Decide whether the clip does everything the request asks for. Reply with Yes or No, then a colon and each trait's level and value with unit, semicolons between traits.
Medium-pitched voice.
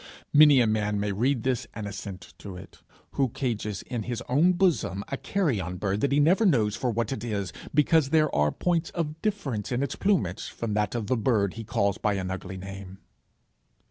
No: low, 115 Hz